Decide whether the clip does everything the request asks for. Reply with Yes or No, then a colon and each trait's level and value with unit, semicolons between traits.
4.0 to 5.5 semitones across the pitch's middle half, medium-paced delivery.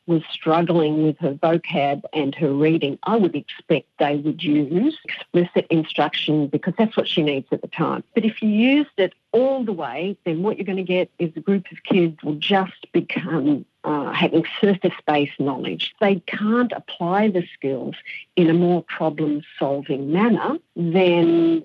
Yes: average, 4.5 semitones; average, 170 wpm